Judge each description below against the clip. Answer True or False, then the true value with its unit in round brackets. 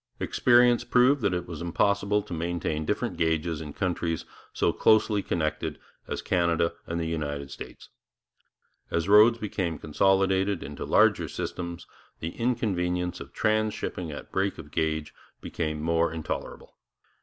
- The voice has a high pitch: False (85 Hz)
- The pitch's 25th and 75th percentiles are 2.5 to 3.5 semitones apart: False (3.9 semitones)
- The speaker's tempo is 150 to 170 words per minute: False (135 wpm)